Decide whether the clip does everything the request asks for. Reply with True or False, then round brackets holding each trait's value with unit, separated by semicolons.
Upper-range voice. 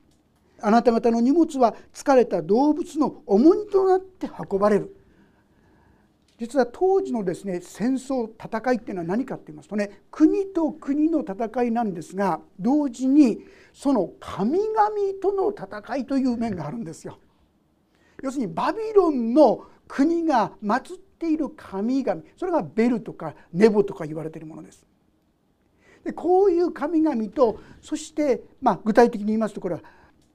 True (255 Hz)